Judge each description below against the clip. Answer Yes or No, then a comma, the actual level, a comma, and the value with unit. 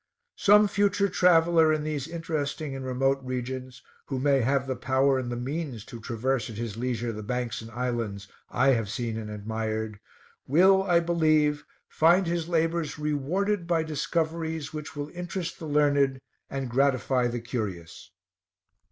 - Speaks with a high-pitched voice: No, low, 135 Hz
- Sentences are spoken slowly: No, average, 155 wpm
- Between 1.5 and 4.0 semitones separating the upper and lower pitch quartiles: No, average, 5.0 semitones